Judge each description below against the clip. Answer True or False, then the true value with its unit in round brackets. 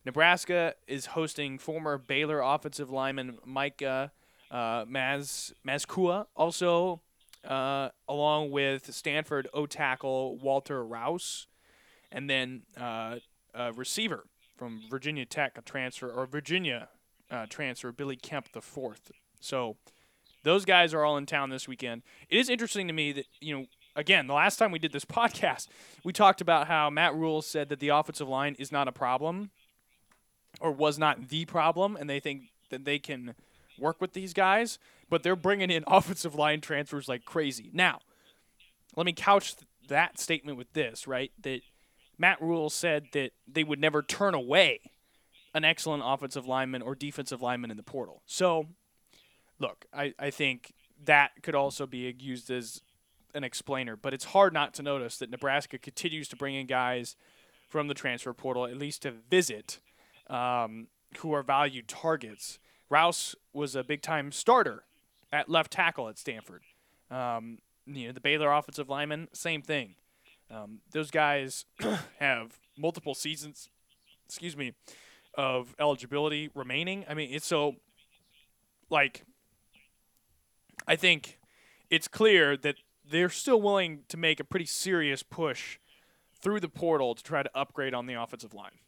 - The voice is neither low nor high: True (145 Hz)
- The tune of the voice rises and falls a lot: False (3.5 semitones)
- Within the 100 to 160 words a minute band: True (155 wpm)